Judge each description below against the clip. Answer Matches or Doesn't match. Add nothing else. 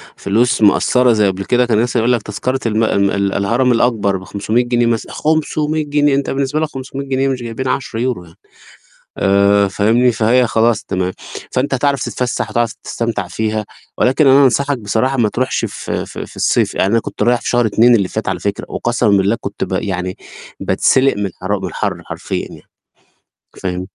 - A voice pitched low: Matches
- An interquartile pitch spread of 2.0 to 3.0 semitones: Doesn't match